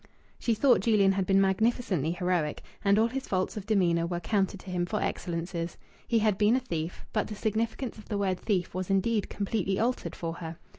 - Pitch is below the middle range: No, high, 195 Hz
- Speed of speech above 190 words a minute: Yes, fast, 205 wpm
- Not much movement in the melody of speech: No, average, 3.5 semitones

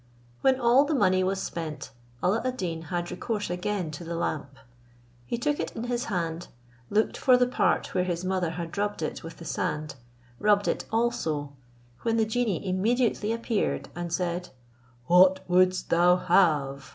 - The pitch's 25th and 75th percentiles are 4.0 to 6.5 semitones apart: Yes, average, 5.0 semitones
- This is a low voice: No, medium, 185 Hz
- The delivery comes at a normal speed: Yes, average, 170 wpm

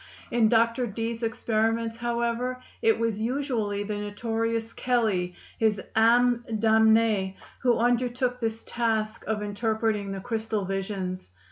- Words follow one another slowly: Yes, slow, 120 wpm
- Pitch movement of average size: No, narrow, 2.0 semitones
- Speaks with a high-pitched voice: Yes, high, 225 Hz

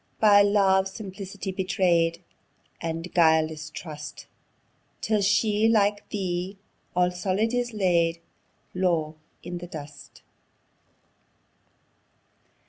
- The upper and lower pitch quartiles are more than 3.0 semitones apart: Yes, average, 3.4 semitones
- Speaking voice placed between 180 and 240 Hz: Yes, medium, 185 Hz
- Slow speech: Yes, slow, 90 wpm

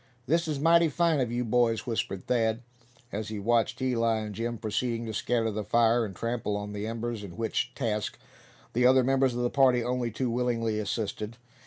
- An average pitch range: No, narrow, 2.2 semitones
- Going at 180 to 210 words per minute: Yes, average, 195 wpm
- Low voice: Yes, low, 115 Hz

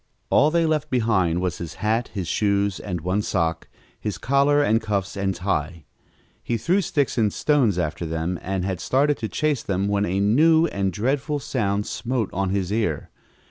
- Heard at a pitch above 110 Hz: No, low, 105 Hz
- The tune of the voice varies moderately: No, wide, 6.1 semitones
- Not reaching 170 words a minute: No, average, 180 wpm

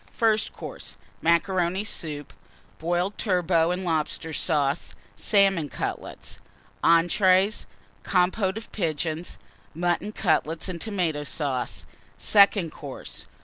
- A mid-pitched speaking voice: Yes, medium, 175 Hz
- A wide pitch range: No, average, 3.3 semitones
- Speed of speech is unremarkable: No, slow, 100 wpm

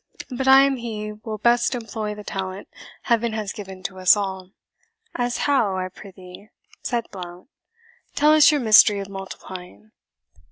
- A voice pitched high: Yes, high, 210 Hz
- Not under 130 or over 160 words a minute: Yes, average, 155 wpm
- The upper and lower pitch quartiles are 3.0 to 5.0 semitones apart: Yes, average, 4.0 semitones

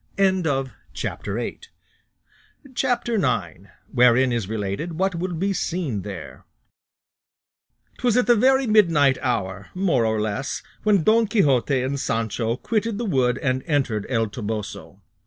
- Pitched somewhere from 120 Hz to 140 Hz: Yes, low, 135 Hz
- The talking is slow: Yes, slow, 120 wpm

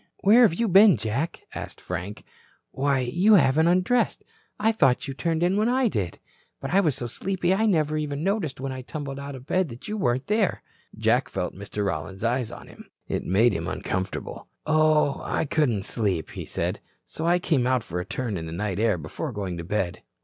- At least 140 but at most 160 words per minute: No, fast, 205 wpm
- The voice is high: No, low, 135 Hz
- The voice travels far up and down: Yes, wide, 8.7 semitones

